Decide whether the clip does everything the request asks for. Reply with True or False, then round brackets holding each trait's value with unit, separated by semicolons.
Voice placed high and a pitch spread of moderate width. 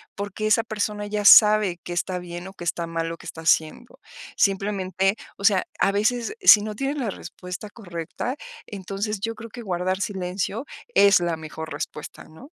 True (195 Hz; 3.3 semitones)